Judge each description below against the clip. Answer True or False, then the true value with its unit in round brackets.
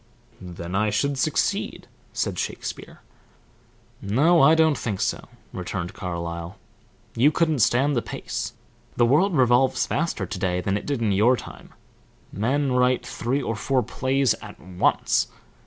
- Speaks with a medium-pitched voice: False (120 Hz)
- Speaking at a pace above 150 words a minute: False (145 wpm)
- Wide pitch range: True (6.1 semitones)